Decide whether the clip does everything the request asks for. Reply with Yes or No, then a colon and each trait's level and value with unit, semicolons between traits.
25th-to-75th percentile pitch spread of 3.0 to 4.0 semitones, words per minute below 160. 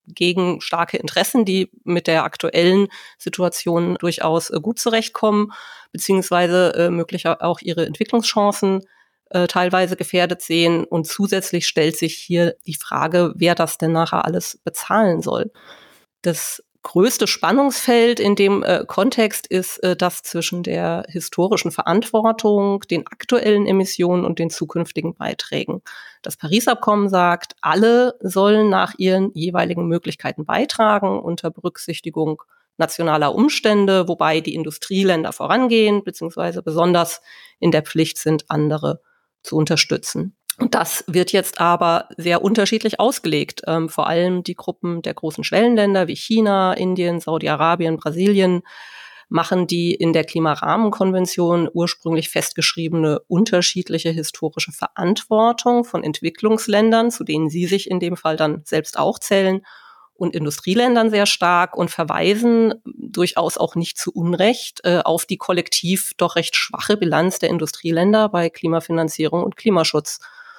Yes: average, 3.6 semitones; slow, 125 wpm